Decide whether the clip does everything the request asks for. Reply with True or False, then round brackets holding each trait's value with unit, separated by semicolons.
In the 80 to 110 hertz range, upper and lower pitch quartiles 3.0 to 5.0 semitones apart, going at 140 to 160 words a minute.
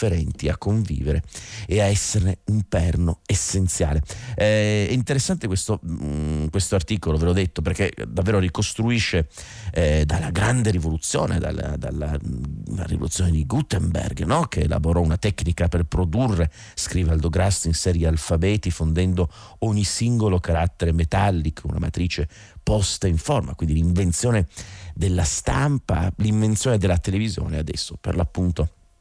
False (90 Hz; 4.1 semitones; 125 wpm)